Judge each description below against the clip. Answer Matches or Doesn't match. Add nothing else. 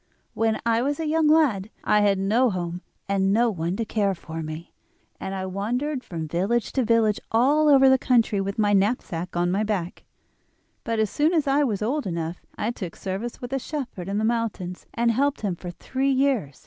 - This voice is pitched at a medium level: Doesn't match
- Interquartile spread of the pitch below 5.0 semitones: Doesn't match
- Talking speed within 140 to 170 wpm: Doesn't match